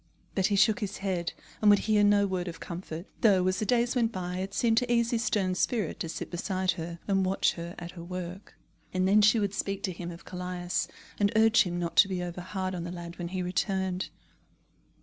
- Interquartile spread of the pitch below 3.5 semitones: Yes, average, 2.7 semitones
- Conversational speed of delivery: No, fast, 230 wpm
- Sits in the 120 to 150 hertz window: No, medium, 185 Hz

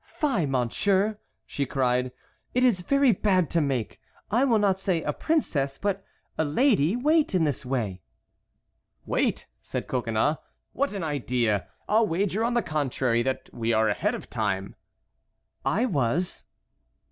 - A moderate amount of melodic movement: No, wide, 8.8 semitones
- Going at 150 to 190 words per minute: No, slow, 135 wpm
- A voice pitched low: No, medium, 160 Hz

